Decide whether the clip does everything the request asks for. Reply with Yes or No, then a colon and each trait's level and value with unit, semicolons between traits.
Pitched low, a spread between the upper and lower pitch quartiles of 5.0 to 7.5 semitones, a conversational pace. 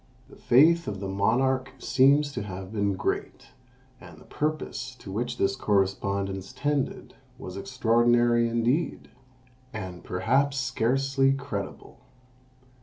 No: low, 120 Hz; wide, 5.4 semitones; slow, 115 wpm